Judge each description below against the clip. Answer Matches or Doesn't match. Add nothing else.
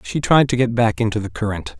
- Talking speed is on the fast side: Matches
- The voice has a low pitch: Matches